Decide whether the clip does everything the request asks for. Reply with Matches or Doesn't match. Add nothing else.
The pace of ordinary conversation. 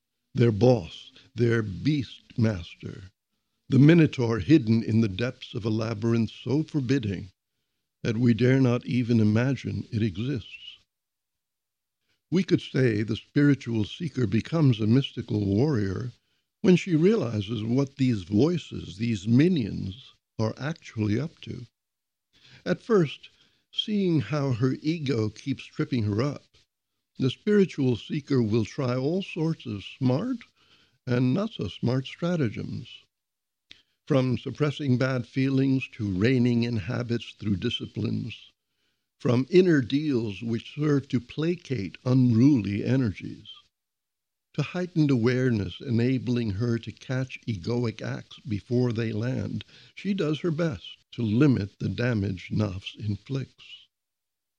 Doesn't match